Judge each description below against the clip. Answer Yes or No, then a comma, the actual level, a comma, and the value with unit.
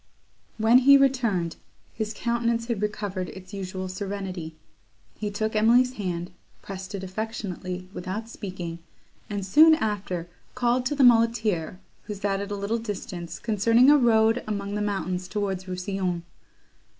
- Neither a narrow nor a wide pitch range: Yes, average, 3.6 semitones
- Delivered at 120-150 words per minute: Yes, average, 140 wpm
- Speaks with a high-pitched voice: Yes, high, 205 Hz